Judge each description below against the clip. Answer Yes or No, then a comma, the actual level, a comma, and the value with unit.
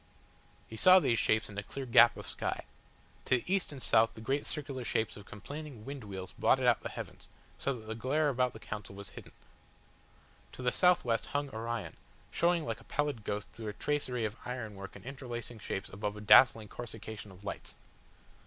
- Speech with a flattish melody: No, average, 4.4 semitones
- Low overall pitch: Yes, low, 115 Hz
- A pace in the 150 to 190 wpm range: No, average, 200 wpm